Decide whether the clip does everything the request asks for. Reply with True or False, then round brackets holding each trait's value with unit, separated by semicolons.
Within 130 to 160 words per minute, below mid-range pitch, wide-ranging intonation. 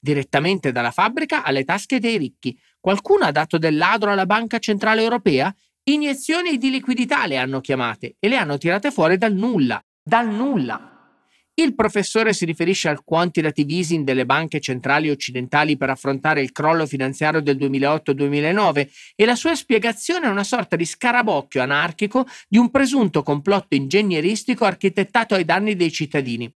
False (155 wpm; 175 Hz; 7.7 semitones)